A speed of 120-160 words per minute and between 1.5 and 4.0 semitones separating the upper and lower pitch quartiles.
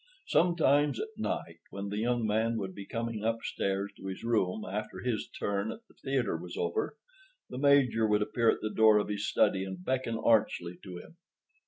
No: average, 190 wpm; average, 3.4 semitones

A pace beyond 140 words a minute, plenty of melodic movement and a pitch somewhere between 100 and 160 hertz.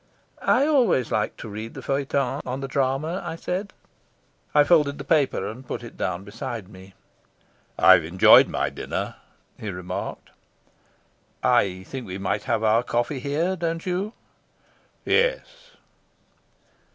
No: slow, 135 wpm; wide, 7.7 semitones; low, 135 Hz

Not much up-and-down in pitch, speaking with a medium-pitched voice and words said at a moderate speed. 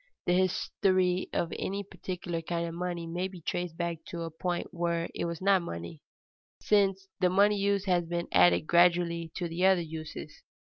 Yes: narrow, 1.8 semitones; medium, 175 Hz; average, 190 wpm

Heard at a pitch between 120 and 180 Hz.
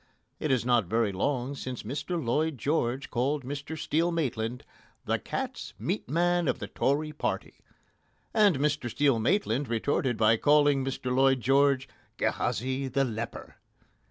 Yes: low, 135 Hz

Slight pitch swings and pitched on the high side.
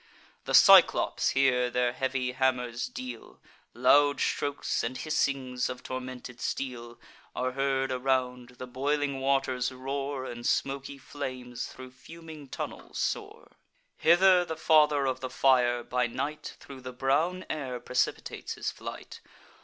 No: narrow, 1.9 semitones; low, 130 Hz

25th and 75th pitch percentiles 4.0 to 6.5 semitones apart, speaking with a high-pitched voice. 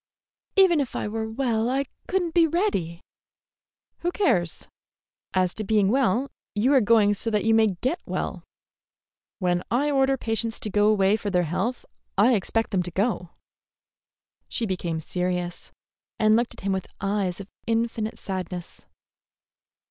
Yes: average, 4.8 semitones; high, 220 Hz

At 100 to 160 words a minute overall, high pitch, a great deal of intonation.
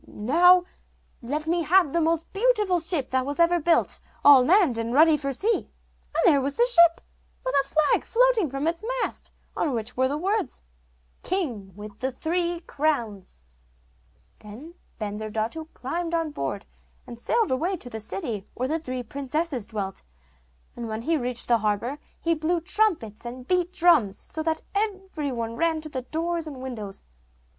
No: average, 170 wpm; very high, 300 Hz; wide, 6.1 semitones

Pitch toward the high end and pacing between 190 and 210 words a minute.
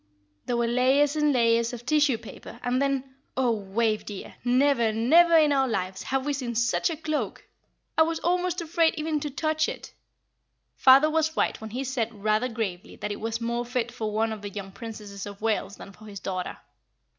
Yes: high, 240 Hz; fast, 205 wpm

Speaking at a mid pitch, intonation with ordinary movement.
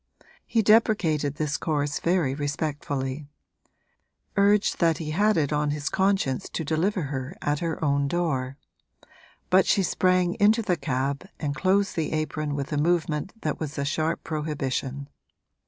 Yes: medium, 155 Hz; average, 4.2 semitones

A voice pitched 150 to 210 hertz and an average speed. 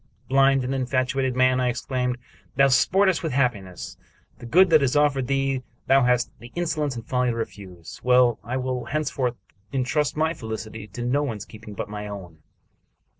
No: low, 125 Hz; average, 175 wpm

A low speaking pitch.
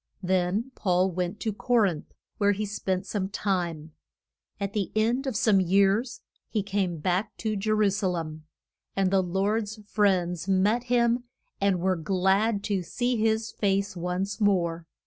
No: high, 195 Hz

